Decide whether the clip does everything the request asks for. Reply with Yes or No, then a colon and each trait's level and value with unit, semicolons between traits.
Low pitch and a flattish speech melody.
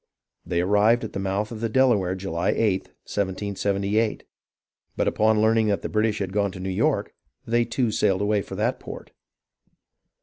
Yes: low, 105 Hz; narrow, 2.2 semitones